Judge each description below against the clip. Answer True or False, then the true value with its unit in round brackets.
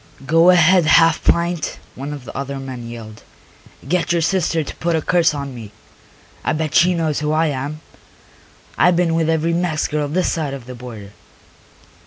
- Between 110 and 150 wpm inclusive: False (185 wpm)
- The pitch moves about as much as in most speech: True (3.5 semitones)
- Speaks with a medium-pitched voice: True (155 Hz)